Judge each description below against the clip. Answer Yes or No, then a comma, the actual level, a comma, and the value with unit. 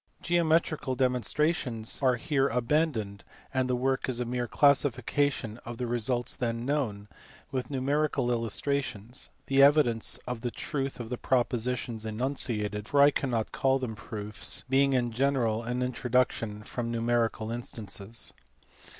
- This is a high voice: No, low, 125 Hz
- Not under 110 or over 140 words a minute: Yes, slow, 135 wpm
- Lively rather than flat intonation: No, average, 2.9 semitones